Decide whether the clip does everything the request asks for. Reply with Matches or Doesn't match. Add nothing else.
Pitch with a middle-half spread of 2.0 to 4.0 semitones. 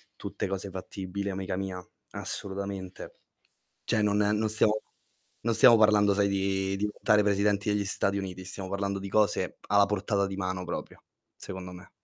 Doesn't match